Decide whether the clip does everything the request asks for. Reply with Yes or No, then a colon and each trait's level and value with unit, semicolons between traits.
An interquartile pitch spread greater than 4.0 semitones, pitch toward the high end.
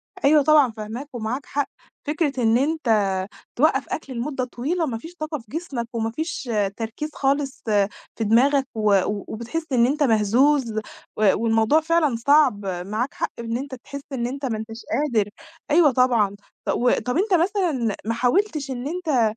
Yes: average, 4.8 semitones; very high, 255 Hz